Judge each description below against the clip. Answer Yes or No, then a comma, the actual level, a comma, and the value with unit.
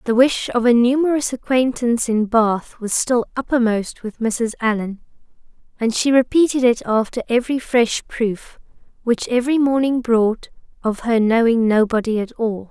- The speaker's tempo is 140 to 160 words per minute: Yes, average, 150 wpm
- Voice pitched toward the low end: No, high, 235 Hz